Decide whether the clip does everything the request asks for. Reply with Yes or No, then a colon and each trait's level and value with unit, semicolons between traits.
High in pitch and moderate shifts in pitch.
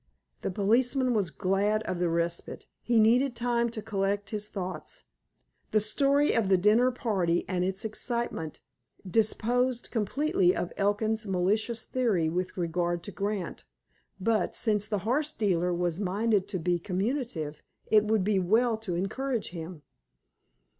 Yes: high, 210 Hz; average, 4.3 semitones